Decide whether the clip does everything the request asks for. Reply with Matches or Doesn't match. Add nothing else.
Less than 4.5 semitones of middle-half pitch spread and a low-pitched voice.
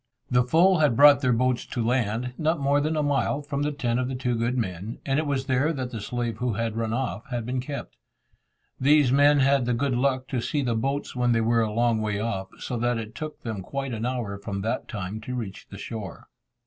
Matches